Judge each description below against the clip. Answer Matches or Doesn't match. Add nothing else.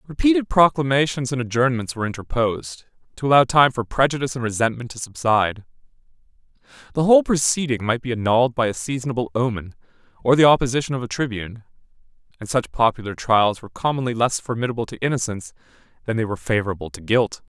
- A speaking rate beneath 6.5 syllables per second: Doesn't match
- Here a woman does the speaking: Doesn't match